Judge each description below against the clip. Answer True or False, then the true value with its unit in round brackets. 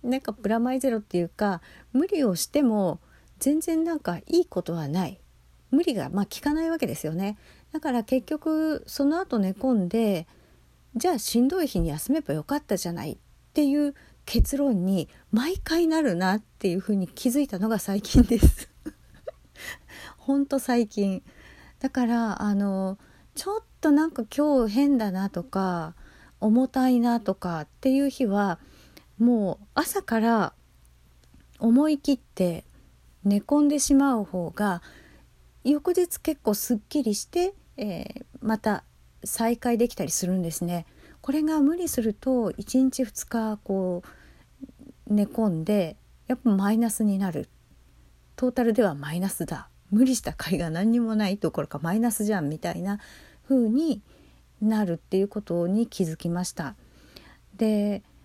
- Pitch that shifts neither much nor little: False (6.1 semitones)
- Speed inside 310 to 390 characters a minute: False (285 characters per minute)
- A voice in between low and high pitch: False (220 Hz)